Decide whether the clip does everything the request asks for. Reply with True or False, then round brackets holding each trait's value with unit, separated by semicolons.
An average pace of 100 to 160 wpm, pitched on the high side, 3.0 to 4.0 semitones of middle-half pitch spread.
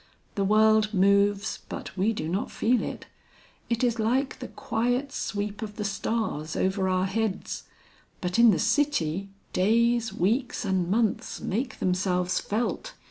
True (145 wpm; 210 Hz; 3.6 semitones)